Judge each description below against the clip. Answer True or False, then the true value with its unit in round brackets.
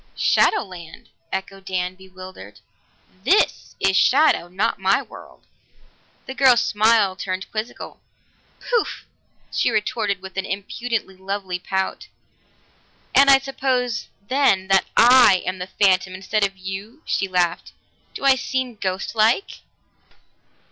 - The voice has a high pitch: True (195 Hz)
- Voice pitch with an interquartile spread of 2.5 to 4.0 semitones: False (4.5 semitones)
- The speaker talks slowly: True (120 wpm)